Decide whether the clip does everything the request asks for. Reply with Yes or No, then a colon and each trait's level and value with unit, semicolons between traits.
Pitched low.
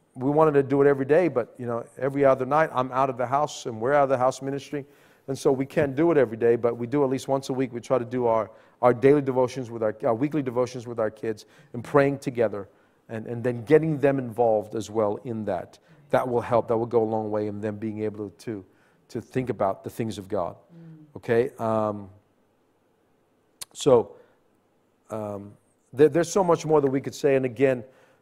Yes: low, 130 Hz